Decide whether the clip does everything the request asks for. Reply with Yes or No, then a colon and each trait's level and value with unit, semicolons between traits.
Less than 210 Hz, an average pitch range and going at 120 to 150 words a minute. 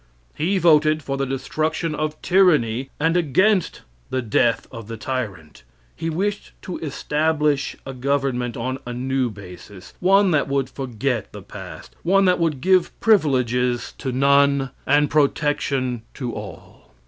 Yes: medium, 140 Hz; average, 4.0 semitones; average, 145 wpm